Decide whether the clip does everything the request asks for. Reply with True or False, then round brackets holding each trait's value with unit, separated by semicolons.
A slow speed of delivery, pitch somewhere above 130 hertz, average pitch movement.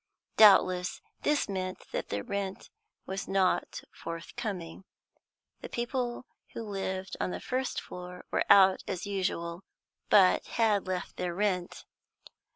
False (125 wpm; 190 Hz; 2.3 semitones)